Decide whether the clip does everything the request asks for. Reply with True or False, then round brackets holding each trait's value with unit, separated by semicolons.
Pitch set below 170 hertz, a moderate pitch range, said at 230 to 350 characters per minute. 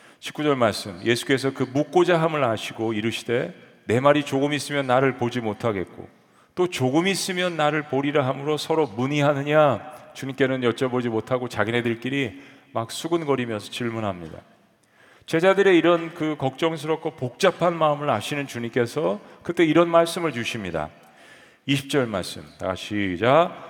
True (135 Hz; 4.8 semitones; 325 characters per minute)